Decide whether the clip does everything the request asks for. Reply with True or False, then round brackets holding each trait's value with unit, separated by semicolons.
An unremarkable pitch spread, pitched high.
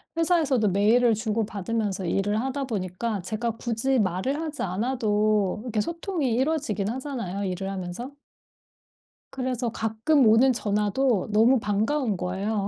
True (4.4 semitones; 220 Hz)